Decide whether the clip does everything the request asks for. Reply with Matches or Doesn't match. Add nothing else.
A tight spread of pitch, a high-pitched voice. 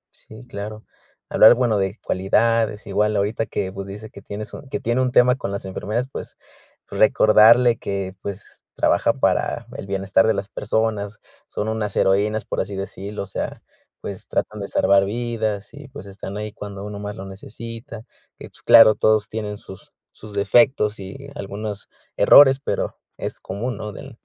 Doesn't match